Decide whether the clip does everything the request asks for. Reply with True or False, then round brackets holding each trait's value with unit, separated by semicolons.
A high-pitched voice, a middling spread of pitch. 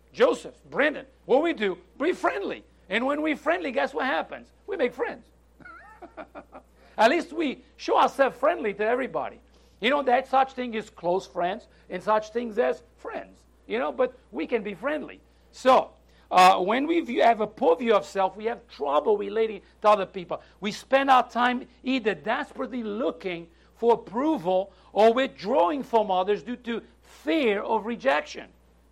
True (235 Hz; 4.9 semitones)